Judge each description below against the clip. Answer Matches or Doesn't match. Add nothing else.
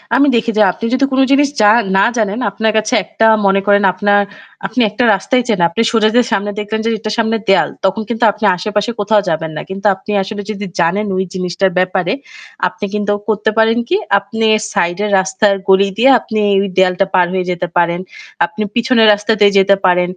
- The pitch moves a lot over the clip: Doesn't match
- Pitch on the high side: Matches